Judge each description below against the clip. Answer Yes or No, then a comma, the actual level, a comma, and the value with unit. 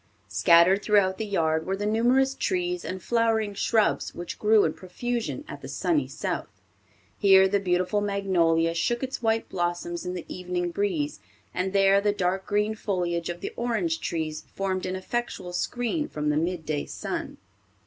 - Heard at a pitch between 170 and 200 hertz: Yes, high, 190 Hz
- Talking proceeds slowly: No, average, 170 wpm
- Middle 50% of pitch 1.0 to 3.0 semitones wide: No, average, 3.9 semitones